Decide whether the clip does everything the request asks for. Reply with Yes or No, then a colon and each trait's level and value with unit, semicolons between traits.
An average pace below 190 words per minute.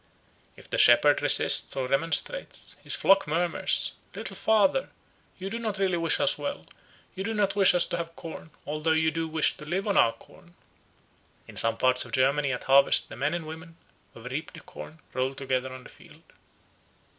No: average, 195 wpm